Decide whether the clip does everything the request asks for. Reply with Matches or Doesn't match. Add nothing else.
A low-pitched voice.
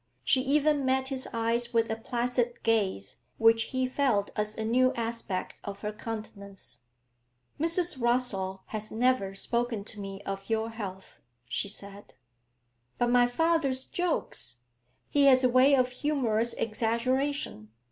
Doesn't match